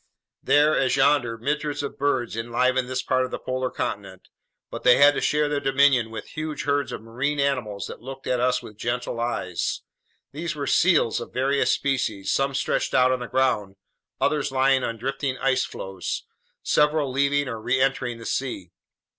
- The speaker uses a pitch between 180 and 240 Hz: No, low, 130 Hz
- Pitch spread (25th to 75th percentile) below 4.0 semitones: Yes, average, 2.8 semitones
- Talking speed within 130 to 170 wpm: No, average, 180 wpm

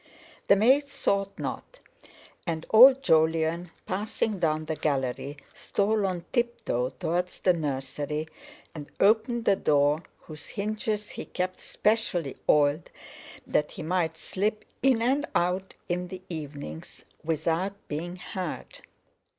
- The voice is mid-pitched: Yes, medium, 180 Hz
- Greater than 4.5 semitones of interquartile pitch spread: Yes, average, 5.2 semitones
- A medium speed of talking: No, slow, 125 wpm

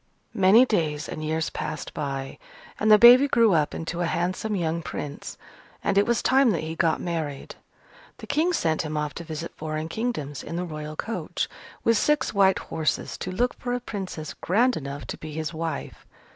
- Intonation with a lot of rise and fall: Yes, wide, 5.9 semitones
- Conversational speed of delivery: Yes, average, 190 wpm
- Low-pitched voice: No, medium, 170 Hz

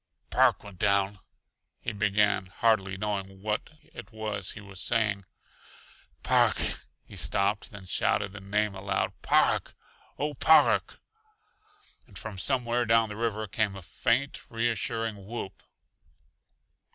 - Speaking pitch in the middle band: No, low, 105 Hz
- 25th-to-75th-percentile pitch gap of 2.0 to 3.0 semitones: Yes, narrow, 2.5 semitones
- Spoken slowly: Yes, slow, 130 wpm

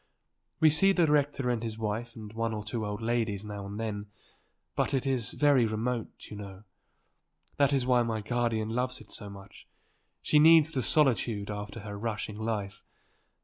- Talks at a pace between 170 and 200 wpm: Yes, average, 180 wpm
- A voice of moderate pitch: No, low, 115 Hz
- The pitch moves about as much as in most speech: Yes, average, 3.5 semitones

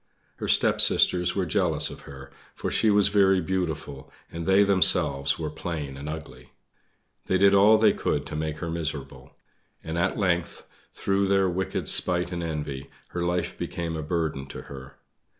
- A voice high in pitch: No, very low, 85 Hz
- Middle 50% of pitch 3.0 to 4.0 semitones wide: Yes, average, 3.7 semitones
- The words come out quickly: No, average, 170 wpm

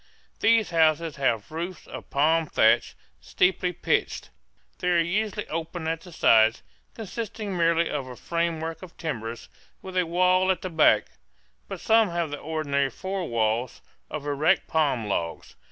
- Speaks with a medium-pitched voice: Yes, medium, 165 Hz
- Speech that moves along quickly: No, average, 155 wpm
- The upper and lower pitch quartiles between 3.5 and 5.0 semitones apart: Yes, average, 4.2 semitones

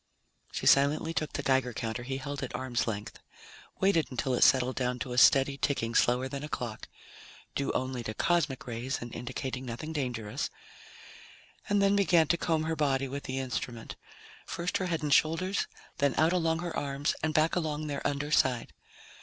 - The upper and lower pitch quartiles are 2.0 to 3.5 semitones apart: No, average, 4.0 semitones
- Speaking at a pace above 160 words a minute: Yes, average, 185 wpm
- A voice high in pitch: No, medium, 140 Hz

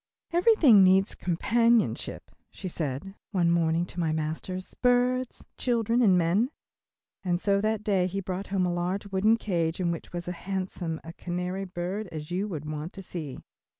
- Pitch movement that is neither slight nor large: Yes, average, 3.3 semitones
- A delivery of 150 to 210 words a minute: Yes, average, 170 wpm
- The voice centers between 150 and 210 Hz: Yes, medium, 185 Hz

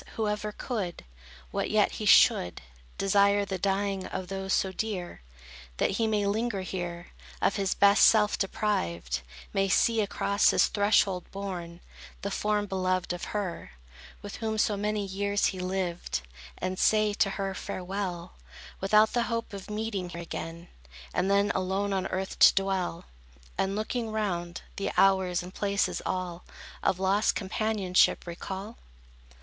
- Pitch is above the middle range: Yes, high, 195 Hz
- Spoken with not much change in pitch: Yes, narrow, 2.1 semitones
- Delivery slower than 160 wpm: Yes, average, 150 wpm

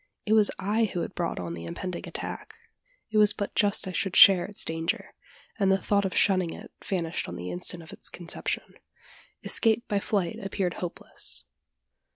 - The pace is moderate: Yes, average, 185 wpm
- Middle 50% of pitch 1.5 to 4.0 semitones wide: Yes, average, 3.4 semitones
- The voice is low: No, high, 190 Hz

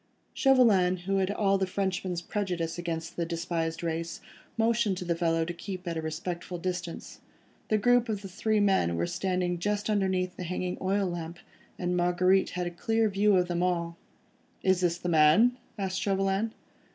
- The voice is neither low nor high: Yes, medium, 180 Hz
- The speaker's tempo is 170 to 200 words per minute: Yes, average, 175 wpm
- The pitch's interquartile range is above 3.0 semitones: No, narrow, 2.5 semitones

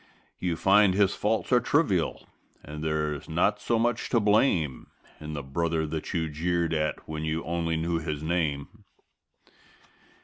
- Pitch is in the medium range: No, very low, 85 Hz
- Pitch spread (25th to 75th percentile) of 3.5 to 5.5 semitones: Yes, average, 4.1 semitones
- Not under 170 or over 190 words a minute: No, average, 150 wpm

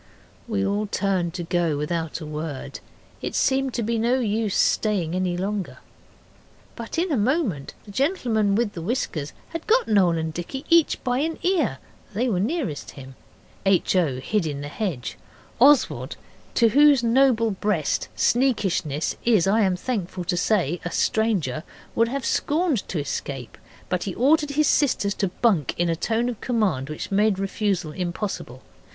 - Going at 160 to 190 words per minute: Yes, average, 165 wpm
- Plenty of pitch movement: Yes, wide, 6.1 semitones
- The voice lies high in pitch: Yes, high, 205 Hz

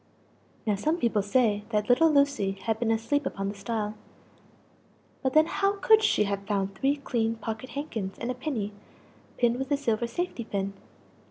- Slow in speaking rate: No, average, 175 wpm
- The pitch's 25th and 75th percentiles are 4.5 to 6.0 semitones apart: Yes, average, 5.3 semitones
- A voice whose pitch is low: No, high, 230 Hz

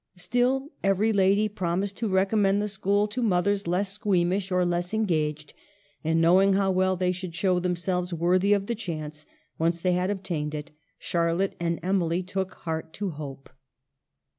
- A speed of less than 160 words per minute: No, average, 165 wpm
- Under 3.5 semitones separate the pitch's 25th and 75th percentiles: Yes, average, 2.7 semitones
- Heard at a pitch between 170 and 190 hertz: Yes, medium, 185 Hz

